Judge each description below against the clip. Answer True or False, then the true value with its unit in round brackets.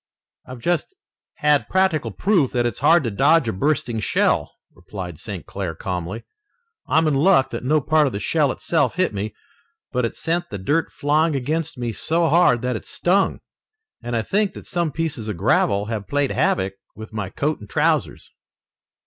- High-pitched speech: False (135 Hz)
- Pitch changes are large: True (6.8 semitones)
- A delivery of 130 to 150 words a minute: False (185 wpm)